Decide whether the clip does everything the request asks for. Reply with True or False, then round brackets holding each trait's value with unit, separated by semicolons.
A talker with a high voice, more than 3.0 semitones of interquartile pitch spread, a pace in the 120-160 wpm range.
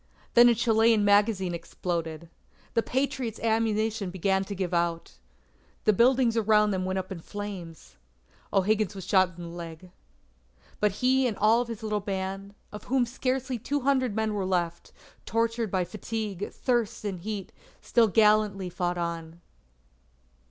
True (205 Hz; 3.6 semitones; 150 wpm)